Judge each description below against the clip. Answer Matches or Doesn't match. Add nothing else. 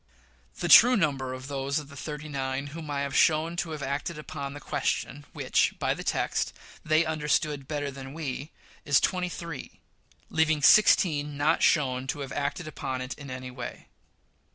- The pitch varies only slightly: Matches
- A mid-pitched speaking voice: Matches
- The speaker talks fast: Doesn't match